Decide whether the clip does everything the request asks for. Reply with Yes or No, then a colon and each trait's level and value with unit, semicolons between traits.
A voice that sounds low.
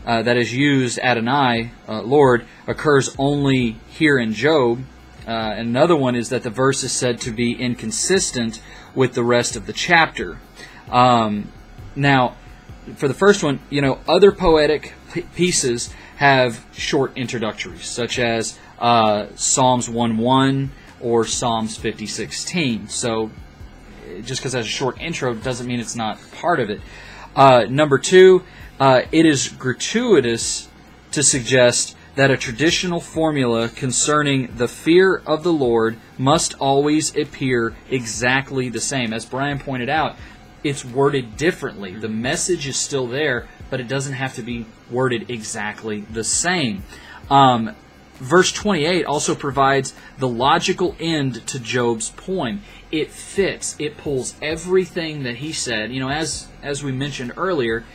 Yes: low, 130 Hz